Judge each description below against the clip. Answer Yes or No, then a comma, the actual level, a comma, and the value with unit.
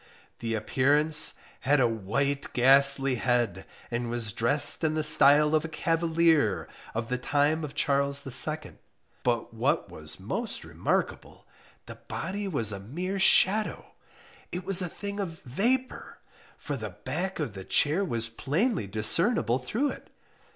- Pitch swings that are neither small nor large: No, wide, 5.7 semitones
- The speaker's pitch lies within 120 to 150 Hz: Yes, medium, 140 Hz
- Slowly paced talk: No, average, 145 wpm